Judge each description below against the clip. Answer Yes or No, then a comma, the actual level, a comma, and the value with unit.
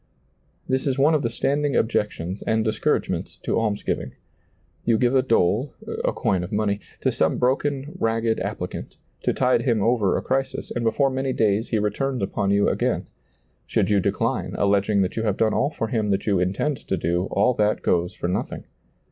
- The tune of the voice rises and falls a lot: No, average, 4.4 semitones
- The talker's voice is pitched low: Yes, low, 110 Hz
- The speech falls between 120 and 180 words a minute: No, average, 195 wpm